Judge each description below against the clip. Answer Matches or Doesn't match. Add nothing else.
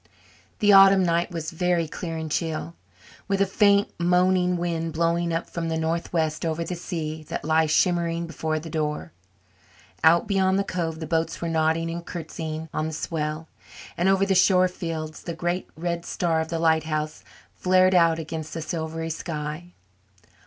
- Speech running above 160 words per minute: Matches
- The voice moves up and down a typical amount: Doesn't match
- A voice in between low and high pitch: Matches